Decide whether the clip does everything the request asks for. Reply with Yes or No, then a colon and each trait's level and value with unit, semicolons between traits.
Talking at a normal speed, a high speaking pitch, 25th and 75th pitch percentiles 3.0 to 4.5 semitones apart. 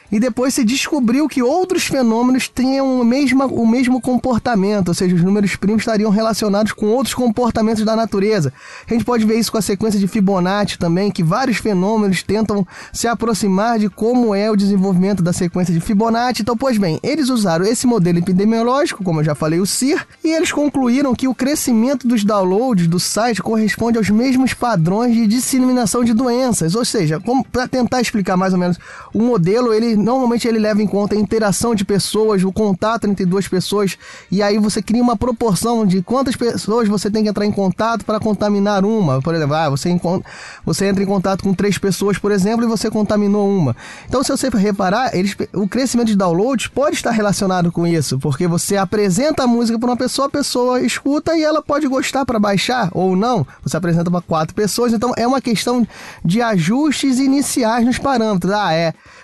No: fast, 195 wpm; high, 220 Hz; average, 4.0 semitones